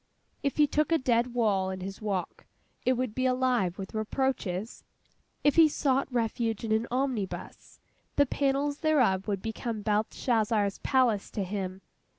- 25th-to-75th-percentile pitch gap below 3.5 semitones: No, average, 4.5 semitones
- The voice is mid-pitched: No, high, 230 Hz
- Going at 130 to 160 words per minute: Yes, average, 155 wpm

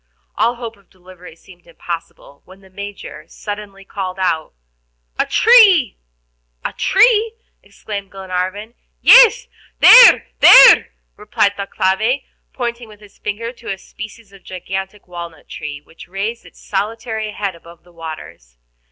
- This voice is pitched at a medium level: No, high, 200 Hz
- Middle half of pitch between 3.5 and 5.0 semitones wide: Yes, average, 4.0 semitones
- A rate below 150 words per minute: Yes, slow, 135 wpm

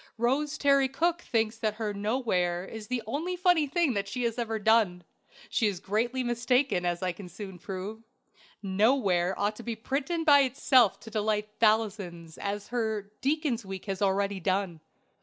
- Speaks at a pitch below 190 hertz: No, high, 220 Hz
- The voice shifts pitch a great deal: No, average, 4.7 semitones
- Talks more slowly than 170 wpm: Yes, average, 160 wpm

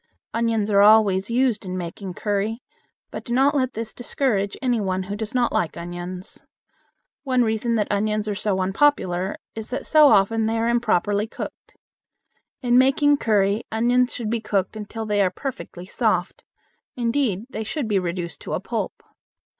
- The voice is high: Yes, high, 220 Hz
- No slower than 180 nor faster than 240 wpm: No, average, 170 wpm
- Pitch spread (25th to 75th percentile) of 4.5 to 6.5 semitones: No, average, 3.4 semitones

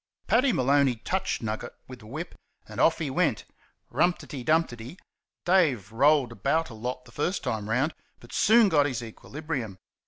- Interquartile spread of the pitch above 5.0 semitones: Yes, wide, 5.5 semitones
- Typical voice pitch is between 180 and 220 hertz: No, medium, 140 Hz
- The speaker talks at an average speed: Yes, average, 185 wpm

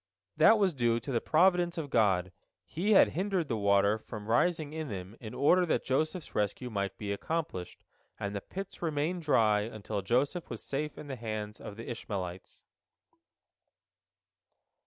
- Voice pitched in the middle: No, low, 120 Hz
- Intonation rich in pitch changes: Yes, wide, 7.5 semitones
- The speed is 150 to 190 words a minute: Yes, average, 160 wpm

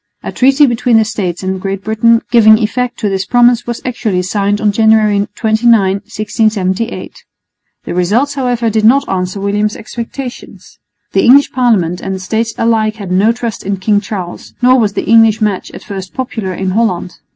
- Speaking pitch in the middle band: No, high, 220 Hz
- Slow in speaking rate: No, average, 175 wpm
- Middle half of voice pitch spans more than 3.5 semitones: No, average, 3.1 semitones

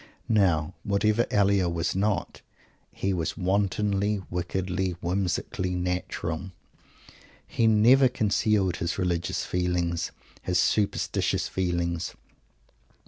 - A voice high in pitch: No, very low, 95 Hz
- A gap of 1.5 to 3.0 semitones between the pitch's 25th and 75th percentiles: Yes, narrow, 2.4 semitones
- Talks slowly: Yes, slow, 90 wpm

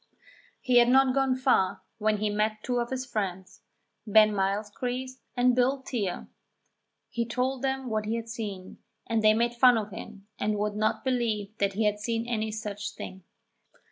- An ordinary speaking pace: Yes, average, 175 wpm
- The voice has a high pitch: Yes, high, 220 Hz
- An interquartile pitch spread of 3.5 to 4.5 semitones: No, average, 3.0 semitones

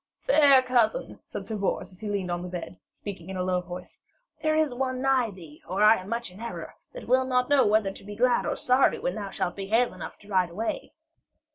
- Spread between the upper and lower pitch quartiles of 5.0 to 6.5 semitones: Yes, wide, 5.4 semitones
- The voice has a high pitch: Yes, high, 215 Hz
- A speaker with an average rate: No, fast, 240 wpm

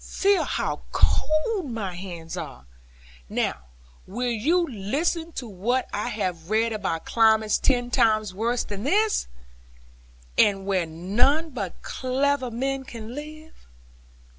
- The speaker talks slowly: Yes, slow, 125 wpm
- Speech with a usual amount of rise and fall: No, wide, 6.0 semitones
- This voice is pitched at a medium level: No, high, 230 Hz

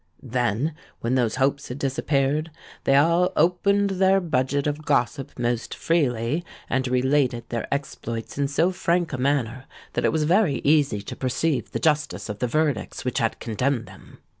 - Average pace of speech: Yes, average, 165 wpm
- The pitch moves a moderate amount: Yes, average, 4.2 semitones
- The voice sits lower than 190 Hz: Yes, medium, 140 Hz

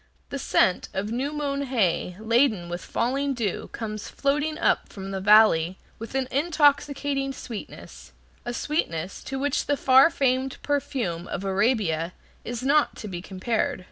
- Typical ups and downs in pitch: No, wide, 6.3 semitones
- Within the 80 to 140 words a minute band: No, average, 150 wpm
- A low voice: No, high, 240 Hz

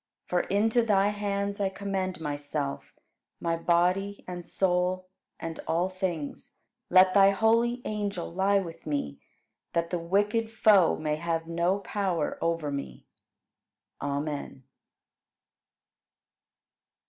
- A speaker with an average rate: No, slow, 110 wpm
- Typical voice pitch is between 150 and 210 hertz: Yes, medium, 185 Hz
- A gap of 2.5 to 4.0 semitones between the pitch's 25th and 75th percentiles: Yes, average, 3.4 semitones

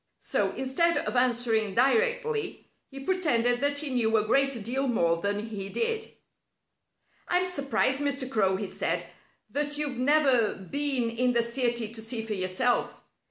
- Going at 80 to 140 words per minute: No, average, 155 wpm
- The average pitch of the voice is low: No, very high, 250 Hz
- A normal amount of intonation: Yes, average, 4.2 semitones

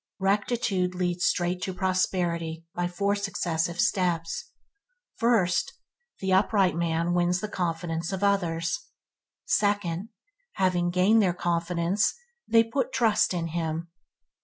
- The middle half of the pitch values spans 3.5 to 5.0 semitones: No, average, 2.8 semitones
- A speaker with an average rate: No, slow, 115 wpm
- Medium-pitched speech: Yes, medium, 180 Hz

